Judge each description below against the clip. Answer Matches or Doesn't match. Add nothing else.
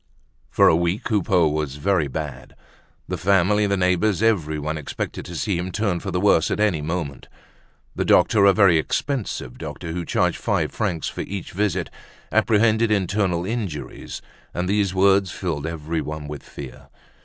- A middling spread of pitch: Matches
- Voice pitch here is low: Matches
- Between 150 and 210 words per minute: Matches